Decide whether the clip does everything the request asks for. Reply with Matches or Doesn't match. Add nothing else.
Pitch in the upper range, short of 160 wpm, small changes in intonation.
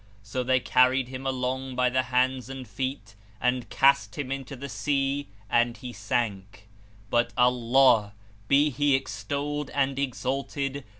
Doesn't match